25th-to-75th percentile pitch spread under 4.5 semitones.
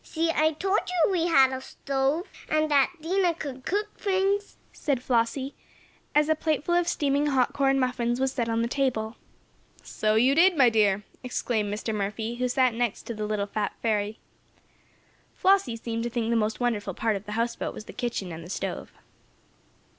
No: wide, 5.6 semitones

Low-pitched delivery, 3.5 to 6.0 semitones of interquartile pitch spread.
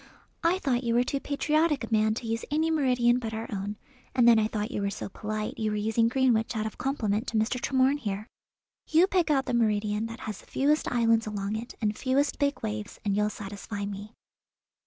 No: high, 225 Hz; average, 3.9 semitones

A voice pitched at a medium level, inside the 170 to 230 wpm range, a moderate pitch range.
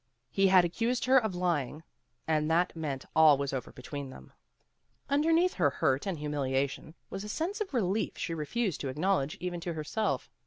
No: medium, 170 Hz; average, 180 wpm; wide, 6.5 semitones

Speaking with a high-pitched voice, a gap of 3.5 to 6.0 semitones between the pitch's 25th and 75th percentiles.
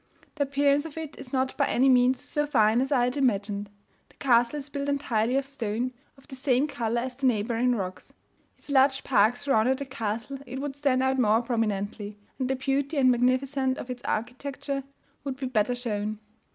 No: very high, 255 Hz; average, 2.9 semitones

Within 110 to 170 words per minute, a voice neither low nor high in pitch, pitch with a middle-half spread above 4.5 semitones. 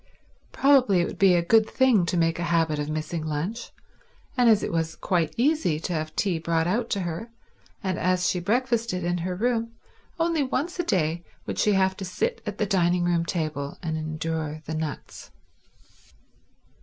No: average, 185 wpm; medium, 175 Hz; wide, 5.5 semitones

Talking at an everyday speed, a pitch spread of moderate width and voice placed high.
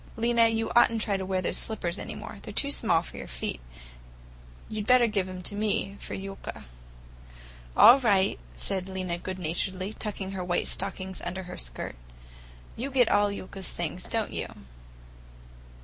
Yes: average, 175 wpm; average, 3.1 semitones; high, 195 Hz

